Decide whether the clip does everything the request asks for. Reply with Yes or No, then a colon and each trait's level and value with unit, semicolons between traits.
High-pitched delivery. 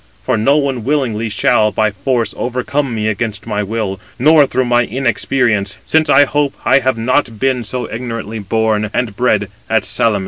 No: low, 120 Hz